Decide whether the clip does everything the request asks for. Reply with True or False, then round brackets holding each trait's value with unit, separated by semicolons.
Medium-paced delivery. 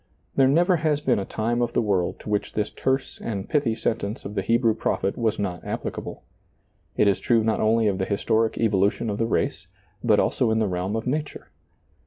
False (210 wpm)